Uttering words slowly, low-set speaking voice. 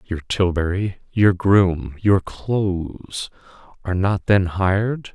Yes: slow, 115 wpm; very low, 95 Hz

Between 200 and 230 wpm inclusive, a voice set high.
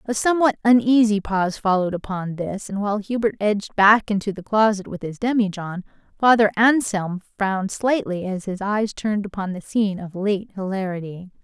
No: average, 170 wpm; high, 205 Hz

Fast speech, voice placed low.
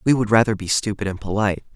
Yes: fast, 240 wpm; low, 105 Hz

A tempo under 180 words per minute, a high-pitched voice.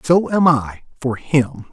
No: average, 140 wpm; medium, 140 Hz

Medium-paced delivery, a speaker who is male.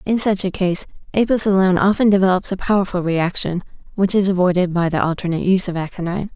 No: average, 190 wpm; female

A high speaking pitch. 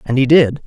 No: low, 135 Hz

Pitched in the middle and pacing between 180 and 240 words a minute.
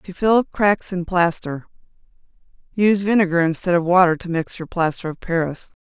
No: medium, 175 Hz; average, 155 wpm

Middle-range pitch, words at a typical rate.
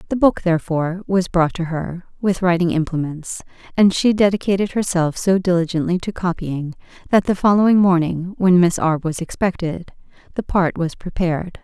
Yes: medium, 180 Hz; average, 160 wpm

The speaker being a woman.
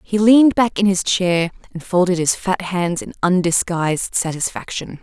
Yes: female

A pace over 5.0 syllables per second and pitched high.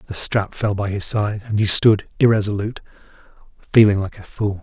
No: 5.6 syllables/s; low, 105 Hz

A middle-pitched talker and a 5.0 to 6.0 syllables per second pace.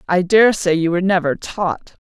Yes: medium, 180 Hz; 5.5 syllables/s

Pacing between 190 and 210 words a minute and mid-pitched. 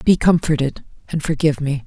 No: average, 160 wpm; medium, 150 Hz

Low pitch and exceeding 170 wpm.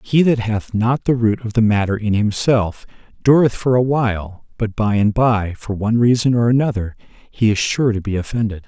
Yes: low, 115 Hz; fast, 205 wpm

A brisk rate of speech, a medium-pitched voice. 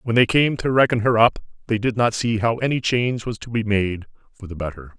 No: fast, 255 wpm; low, 115 Hz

